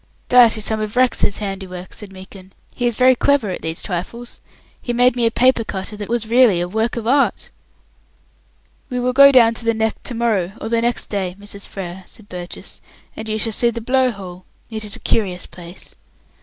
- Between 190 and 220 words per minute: Yes, fast, 205 wpm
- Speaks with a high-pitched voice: Yes, high, 220 Hz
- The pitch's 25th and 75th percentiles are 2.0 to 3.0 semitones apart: No, average, 3.8 semitones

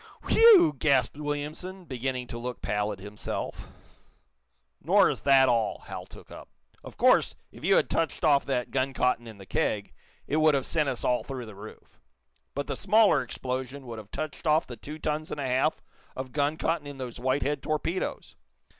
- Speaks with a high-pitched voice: No, low, 135 Hz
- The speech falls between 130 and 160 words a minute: No, average, 185 wpm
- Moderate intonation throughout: Yes, average, 3.7 semitones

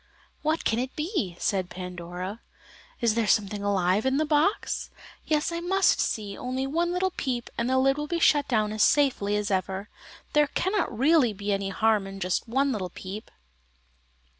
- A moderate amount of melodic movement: No, wide, 6.9 semitones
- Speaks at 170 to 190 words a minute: Yes, average, 185 wpm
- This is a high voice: Yes, high, 230 Hz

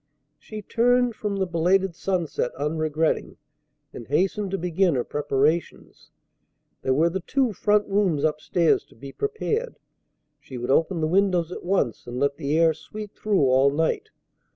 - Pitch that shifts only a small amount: No, average, 5.1 semitones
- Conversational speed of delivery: Yes, average, 160 wpm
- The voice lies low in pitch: No, medium, 170 Hz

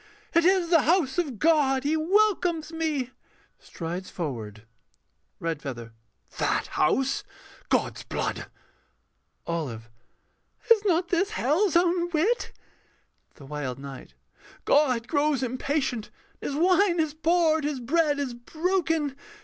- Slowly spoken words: Yes, slow, 120 wpm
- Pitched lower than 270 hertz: No, very high, 300 Hz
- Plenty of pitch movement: Yes, wide, 6.6 semitones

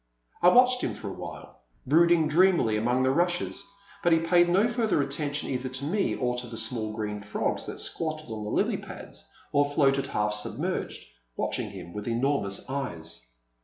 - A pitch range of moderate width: No, wide, 7.4 semitones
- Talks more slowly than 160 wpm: No, average, 180 wpm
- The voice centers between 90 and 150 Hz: Yes, low, 135 Hz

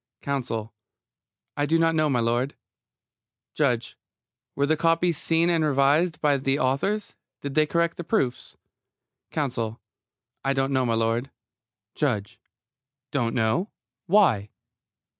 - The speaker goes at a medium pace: No, slow, 120 wpm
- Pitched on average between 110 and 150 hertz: Yes, medium, 140 Hz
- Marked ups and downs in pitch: No, average, 5.0 semitones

